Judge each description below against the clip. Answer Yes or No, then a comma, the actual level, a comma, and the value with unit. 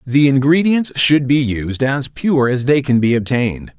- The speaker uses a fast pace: No, average, 190 wpm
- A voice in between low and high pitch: No, low, 130 Hz